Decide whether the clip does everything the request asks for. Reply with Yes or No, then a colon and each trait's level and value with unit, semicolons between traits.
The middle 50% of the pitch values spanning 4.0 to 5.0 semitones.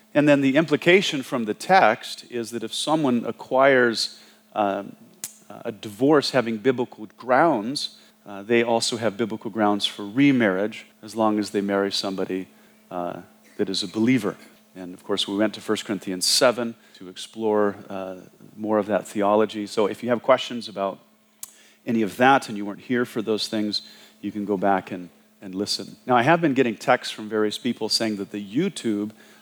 No: average, 3.1 semitones